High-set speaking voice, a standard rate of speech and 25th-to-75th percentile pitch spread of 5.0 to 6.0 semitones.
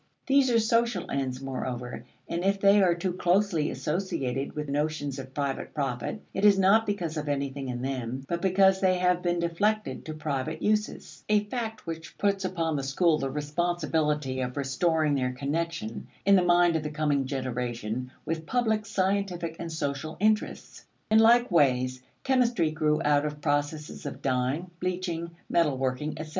No: medium, 160 Hz; average, 170 wpm; wide, 5.4 semitones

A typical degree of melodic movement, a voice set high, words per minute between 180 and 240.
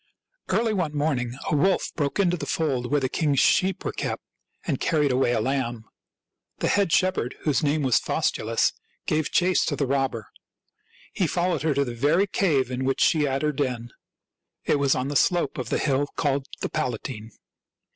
No: average, 3.5 semitones; medium, 140 Hz; average, 190 wpm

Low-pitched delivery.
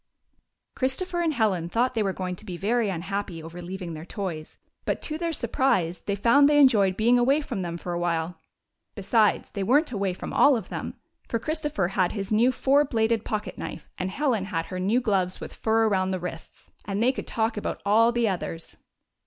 No: high, 210 Hz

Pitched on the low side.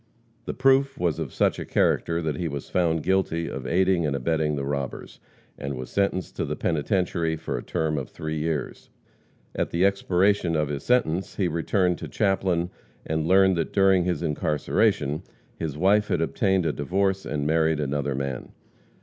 Yes: very low, 85 Hz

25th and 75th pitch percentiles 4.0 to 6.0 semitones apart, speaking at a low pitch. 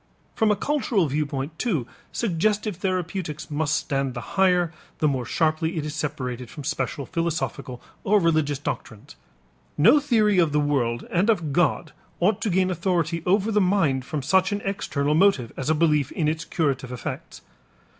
No: average, 4.9 semitones; medium, 160 Hz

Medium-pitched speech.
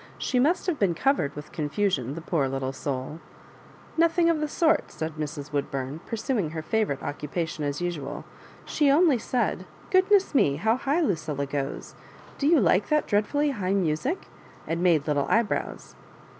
Yes: medium, 175 Hz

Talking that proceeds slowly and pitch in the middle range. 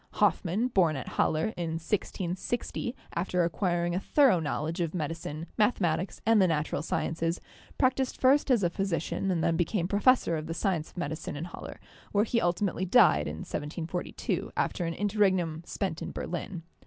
No: average, 165 wpm; medium, 175 Hz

